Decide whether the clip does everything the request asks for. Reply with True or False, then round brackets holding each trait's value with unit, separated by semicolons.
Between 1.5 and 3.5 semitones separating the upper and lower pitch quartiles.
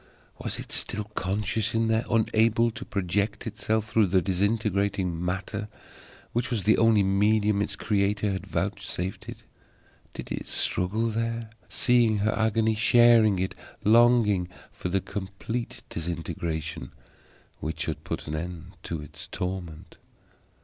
True (3.2 semitones)